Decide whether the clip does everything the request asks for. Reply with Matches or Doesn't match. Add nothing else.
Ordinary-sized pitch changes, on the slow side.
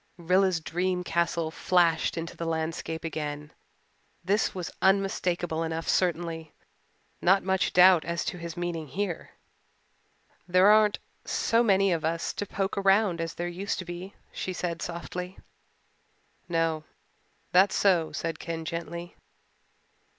Doesn't match